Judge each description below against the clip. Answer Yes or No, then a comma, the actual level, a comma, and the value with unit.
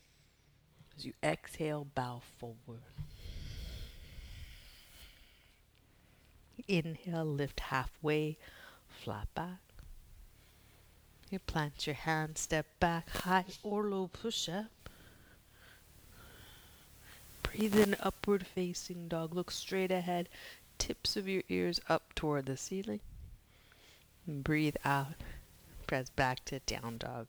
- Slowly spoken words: Yes, slow, 100 wpm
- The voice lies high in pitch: No, medium, 150 Hz